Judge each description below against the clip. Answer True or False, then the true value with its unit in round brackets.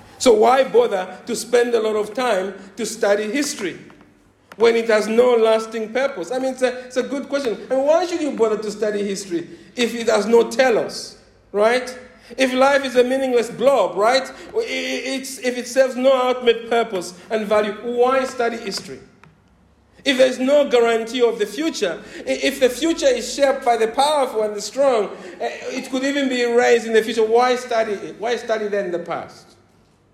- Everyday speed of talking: True (185 wpm)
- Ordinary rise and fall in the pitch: True (3.3 semitones)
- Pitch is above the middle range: True (240 Hz)